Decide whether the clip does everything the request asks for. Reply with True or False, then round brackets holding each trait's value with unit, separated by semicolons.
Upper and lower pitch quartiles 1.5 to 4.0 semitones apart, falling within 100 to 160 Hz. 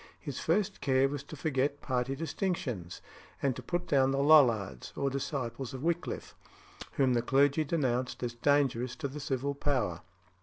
True (2.6 semitones; 135 Hz)